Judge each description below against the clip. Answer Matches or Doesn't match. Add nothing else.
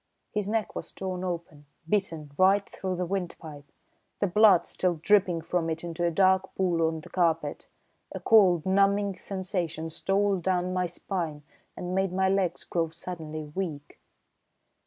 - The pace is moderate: Matches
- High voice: Doesn't match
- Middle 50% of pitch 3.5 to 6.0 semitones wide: Doesn't match